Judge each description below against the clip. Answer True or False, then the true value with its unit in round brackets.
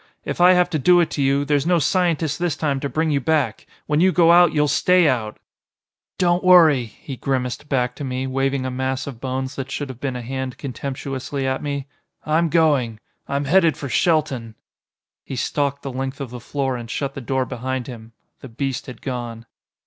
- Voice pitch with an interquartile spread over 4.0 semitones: False (3.0 semitones)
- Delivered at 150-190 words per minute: False (205 wpm)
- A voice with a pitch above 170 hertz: False (135 Hz)